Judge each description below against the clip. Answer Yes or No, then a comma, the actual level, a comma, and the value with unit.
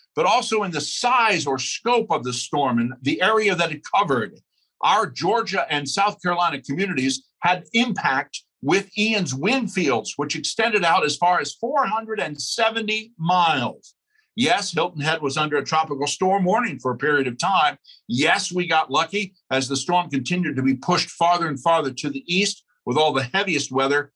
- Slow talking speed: No, average, 180 wpm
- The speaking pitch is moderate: Yes, medium, 170 Hz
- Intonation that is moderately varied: No, wide, 6.1 semitones